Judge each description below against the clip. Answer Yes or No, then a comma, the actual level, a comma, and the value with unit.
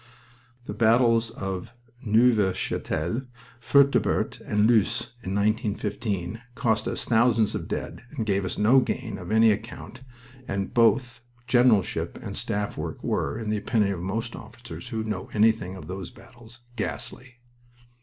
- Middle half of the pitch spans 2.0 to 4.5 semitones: Yes, average, 2.7 semitones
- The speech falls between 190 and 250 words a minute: No, average, 145 wpm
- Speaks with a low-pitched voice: Yes, low, 110 Hz